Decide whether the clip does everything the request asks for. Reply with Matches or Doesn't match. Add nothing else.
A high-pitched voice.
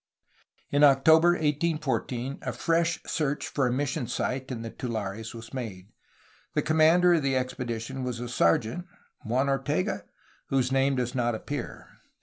Doesn't match